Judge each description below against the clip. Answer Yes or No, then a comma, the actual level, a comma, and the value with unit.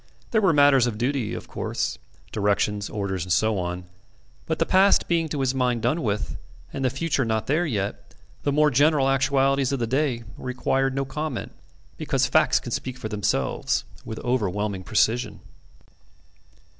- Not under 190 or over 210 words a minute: No, average, 165 wpm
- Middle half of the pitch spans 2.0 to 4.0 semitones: No, average, 4.8 semitones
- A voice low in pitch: Yes, low, 125 Hz